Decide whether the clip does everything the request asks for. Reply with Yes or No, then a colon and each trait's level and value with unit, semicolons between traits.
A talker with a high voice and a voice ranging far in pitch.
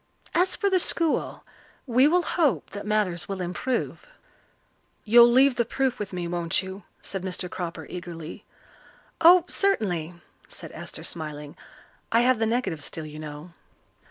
Yes: high, 195 Hz; wide, 7.0 semitones